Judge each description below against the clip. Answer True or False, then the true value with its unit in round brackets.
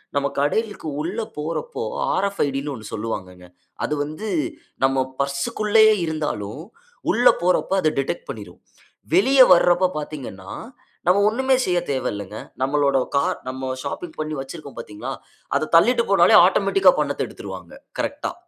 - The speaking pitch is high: False (155 Hz)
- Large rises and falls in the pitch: True (6.0 semitones)